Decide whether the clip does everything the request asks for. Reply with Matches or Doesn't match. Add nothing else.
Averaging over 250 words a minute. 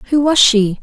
Doesn't match